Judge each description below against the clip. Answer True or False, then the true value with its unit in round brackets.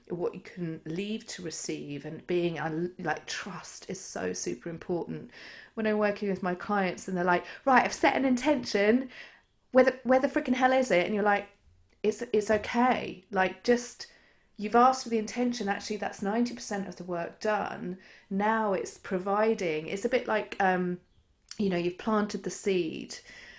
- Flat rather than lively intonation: False (4.6 semitones)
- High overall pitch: True (205 Hz)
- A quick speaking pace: False (180 wpm)